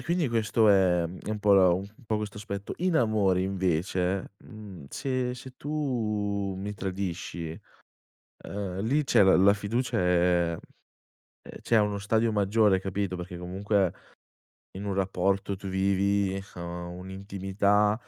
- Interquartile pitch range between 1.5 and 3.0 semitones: Yes, narrow, 2.4 semitones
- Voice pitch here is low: Yes, low, 100 Hz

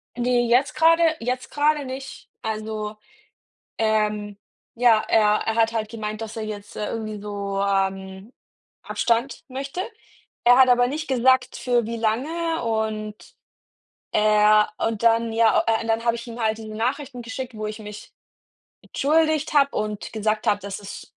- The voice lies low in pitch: No, high, 225 Hz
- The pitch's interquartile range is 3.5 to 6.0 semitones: No, average, 2.9 semitones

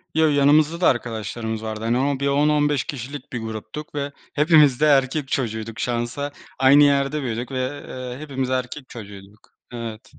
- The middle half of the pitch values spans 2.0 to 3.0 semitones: No, average, 3.8 semitones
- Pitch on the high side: No, low, 130 Hz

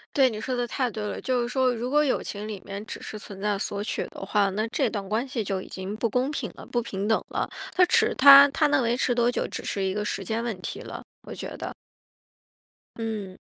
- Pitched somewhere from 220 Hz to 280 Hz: Yes, high, 225 Hz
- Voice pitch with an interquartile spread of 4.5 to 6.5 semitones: No, average, 3.8 semitones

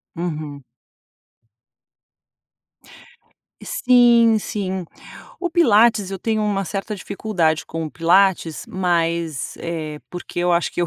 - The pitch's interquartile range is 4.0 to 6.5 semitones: Yes, average, 4.3 semitones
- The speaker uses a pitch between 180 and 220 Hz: Yes, medium, 185 Hz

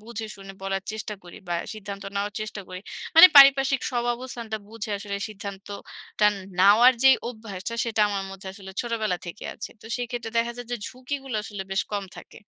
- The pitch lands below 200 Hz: No, high, 215 Hz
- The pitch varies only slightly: No, average, 3.2 semitones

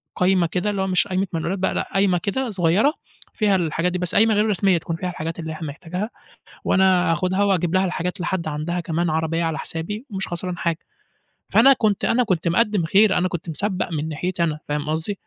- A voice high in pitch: No, medium, 180 Hz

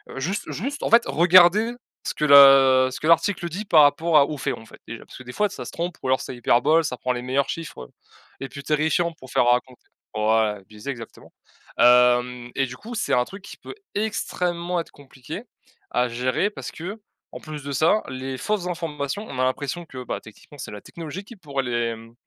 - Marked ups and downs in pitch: Yes, wide, 5.7 semitones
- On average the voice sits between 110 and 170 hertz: Yes, medium, 140 Hz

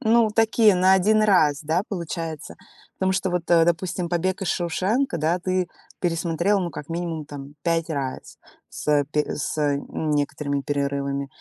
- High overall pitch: No, medium, 170 Hz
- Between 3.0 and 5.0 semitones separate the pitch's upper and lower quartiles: Yes, average, 3.9 semitones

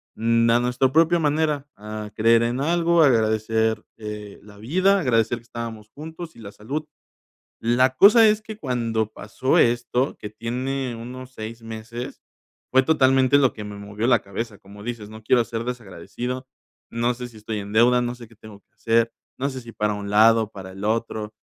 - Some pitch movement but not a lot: Yes, average, 3.1 semitones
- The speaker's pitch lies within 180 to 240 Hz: No, low, 115 Hz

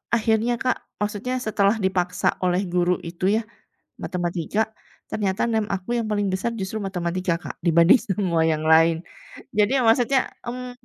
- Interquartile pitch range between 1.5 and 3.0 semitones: No, average, 3.8 semitones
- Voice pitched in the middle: No, high, 195 Hz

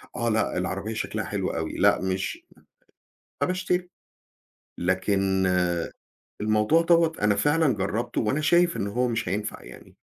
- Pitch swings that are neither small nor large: No, wide, 8.3 semitones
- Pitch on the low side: Yes, low, 110 Hz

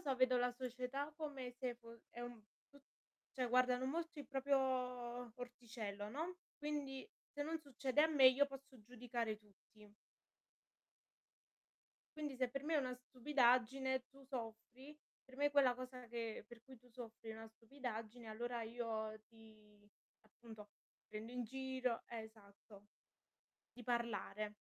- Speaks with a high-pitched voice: Yes, high, 245 Hz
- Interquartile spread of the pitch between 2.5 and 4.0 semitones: Yes, average, 3.0 semitones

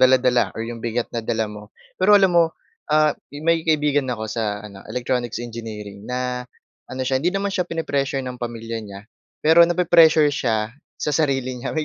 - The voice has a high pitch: No, low, 125 Hz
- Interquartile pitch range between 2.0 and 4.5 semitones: No, average, 5.0 semitones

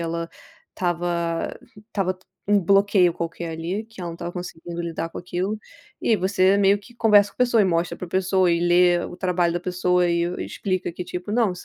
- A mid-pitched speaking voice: Yes, medium, 180 Hz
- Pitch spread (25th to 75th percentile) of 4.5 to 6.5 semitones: No, narrow, 2.5 semitones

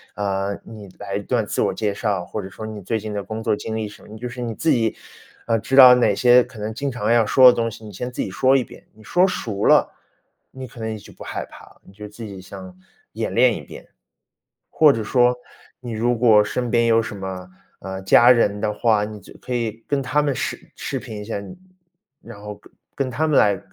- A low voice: Yes, low, 110 Hz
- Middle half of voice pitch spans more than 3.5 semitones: No, average, 3.0 semitones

